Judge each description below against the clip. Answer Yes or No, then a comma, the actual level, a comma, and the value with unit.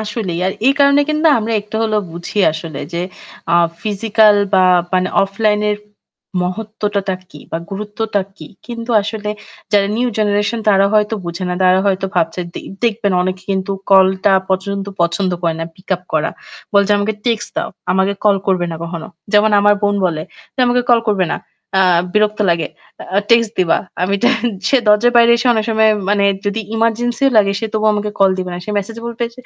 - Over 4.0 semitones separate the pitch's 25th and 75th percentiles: No, average, 2.8 semitones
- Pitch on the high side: Yes, high, 205 Hz